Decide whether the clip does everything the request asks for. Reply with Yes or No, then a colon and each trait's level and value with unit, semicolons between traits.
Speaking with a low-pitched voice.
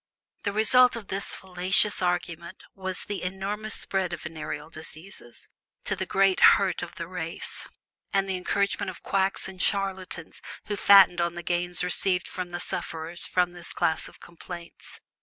No: medium, 185 Hz